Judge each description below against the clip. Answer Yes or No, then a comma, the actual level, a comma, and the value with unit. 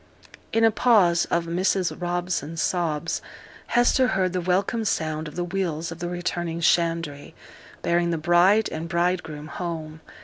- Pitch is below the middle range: No, medium, 175 Hz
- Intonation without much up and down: Yes, narrow, 1.9 semitones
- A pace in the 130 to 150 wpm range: Yes, average, 145 wpm